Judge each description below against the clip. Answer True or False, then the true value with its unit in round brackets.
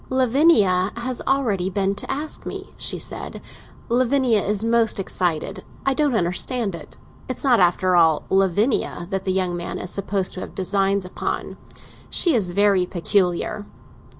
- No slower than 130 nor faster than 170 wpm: True (150 wpm)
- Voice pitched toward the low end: False (200 Hz)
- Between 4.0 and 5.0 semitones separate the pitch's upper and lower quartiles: True (4.6 semitones)